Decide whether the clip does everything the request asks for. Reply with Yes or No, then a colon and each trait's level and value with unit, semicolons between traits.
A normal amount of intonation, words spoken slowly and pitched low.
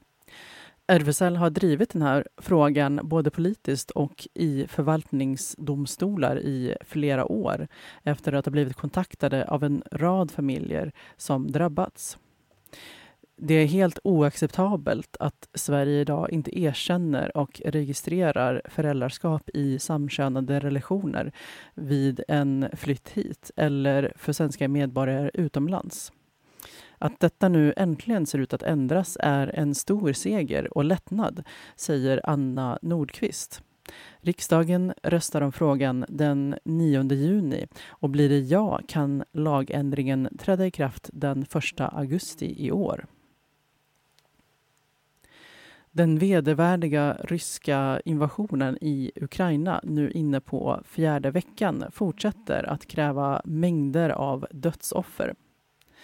No: average, 3.3 semitones; slow, 110 wpm; medium, 150 Hz